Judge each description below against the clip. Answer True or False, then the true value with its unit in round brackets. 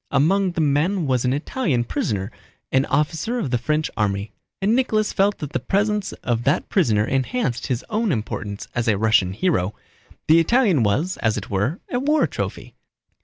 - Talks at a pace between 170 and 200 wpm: True (175 wpm)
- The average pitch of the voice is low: False (145 Hz)